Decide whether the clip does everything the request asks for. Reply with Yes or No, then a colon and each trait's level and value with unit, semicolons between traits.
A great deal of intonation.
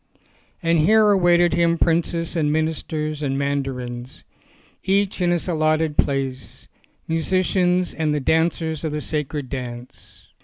No: average, 3.4 semitones